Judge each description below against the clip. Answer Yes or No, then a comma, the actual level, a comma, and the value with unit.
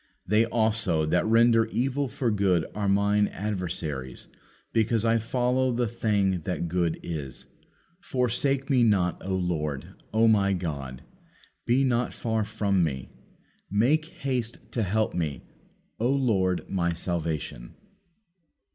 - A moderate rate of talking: No, slow, 130 wpm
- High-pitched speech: No, low, 105 Hz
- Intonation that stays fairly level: No, average, 5.0 semitones